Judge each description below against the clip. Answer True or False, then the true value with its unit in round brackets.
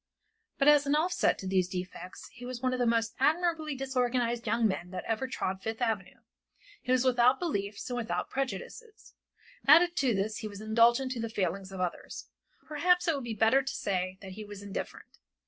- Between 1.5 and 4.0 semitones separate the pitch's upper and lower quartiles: False (5.0 semitones)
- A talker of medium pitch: False (235 Hz)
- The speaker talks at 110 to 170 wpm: False (200 wpm)